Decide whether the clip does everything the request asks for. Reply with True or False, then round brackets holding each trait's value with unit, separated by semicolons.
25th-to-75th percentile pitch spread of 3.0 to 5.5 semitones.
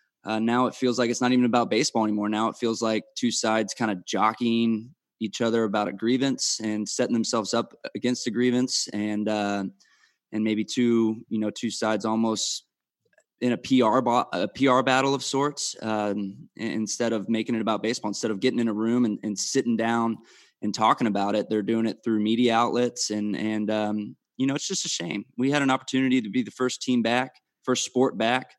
False (2.5 semitones)